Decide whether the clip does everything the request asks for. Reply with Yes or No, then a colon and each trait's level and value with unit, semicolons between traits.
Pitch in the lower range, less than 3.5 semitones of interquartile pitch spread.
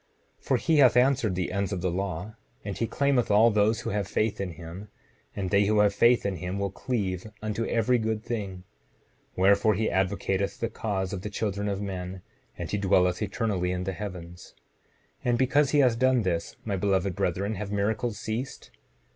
Yes: low, 100 Hz; average, 3.0 semitones